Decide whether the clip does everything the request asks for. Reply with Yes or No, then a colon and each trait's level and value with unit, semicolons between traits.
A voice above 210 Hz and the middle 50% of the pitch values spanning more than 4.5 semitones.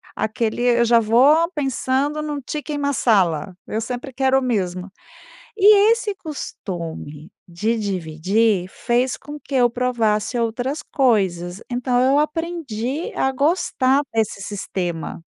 Yes: high, 240 Hz; wide, 5.6 semitones